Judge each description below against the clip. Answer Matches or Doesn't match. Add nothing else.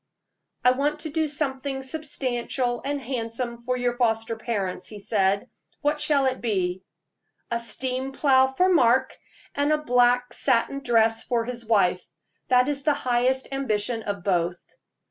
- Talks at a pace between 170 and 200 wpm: Doesn't match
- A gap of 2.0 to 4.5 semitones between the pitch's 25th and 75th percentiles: Matches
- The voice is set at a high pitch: Matches